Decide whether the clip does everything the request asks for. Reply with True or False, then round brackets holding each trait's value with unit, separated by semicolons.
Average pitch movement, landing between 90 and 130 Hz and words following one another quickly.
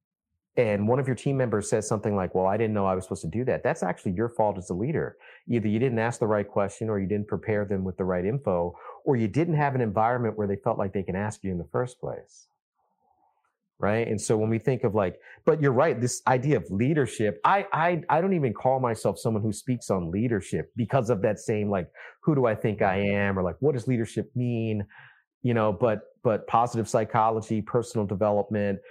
True (3.7 semitones; 110 Hz; 230 wpm)